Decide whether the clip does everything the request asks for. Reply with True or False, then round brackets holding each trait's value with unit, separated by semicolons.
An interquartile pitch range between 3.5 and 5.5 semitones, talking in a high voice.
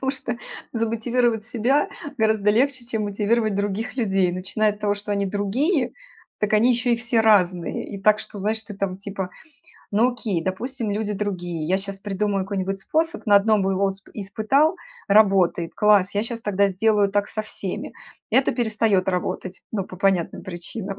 False (2.7 semitones; 205 Hz)